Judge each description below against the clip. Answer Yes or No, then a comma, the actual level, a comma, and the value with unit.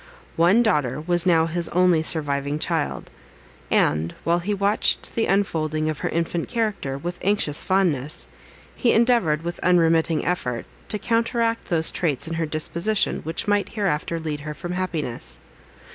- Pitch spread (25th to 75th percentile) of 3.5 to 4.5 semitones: Yes, average, 4.0 semitones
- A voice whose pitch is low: No, medium, 170 Hz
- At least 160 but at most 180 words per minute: No, average, 150 wpm